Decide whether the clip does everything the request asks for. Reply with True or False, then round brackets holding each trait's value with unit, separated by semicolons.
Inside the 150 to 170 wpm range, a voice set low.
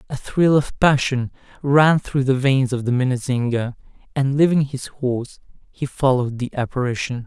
True (155 wpm; 130 Hz)